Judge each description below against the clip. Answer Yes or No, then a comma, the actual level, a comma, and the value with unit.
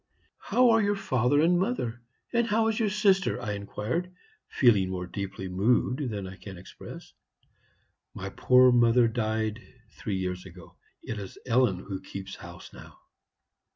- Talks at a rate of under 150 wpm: No, average, 155 wpm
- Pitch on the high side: No, low, 115 Hz